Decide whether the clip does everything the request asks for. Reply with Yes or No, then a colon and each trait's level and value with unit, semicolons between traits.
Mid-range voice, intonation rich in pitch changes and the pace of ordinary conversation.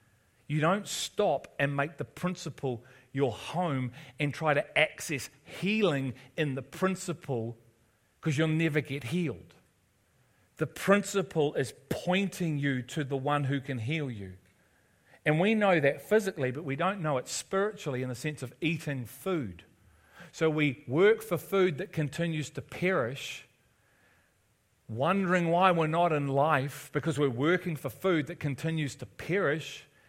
No: medium, 145 Hz; average, 5.0 semitones; average, 150 wpm